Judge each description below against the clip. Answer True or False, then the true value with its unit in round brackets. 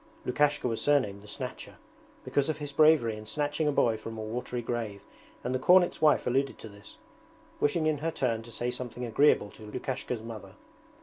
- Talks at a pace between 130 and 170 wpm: False (190 wpm)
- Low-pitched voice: True (125 Hz)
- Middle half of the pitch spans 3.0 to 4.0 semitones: False (4.7 semitones)